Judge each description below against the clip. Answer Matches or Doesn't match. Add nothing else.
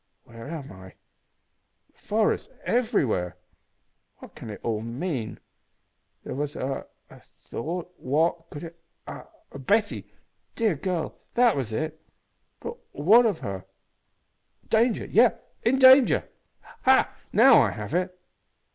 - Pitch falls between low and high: Matches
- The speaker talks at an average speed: Doesn't match